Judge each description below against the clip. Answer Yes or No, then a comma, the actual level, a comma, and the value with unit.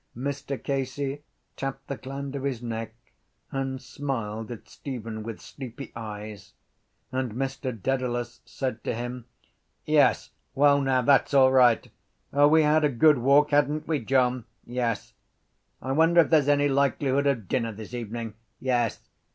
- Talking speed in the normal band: Yes, average, 150 wpm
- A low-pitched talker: Yes, low, 130 Hz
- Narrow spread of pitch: No, average, 3.0 semitones